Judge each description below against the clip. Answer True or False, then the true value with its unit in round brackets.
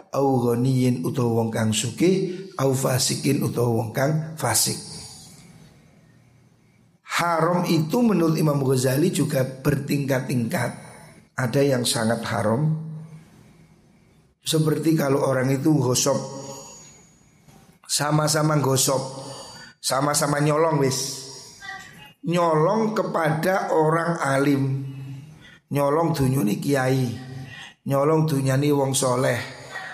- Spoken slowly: True (75 wpm)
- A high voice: False (140 Hz)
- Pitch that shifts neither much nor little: True (3.2 semitones)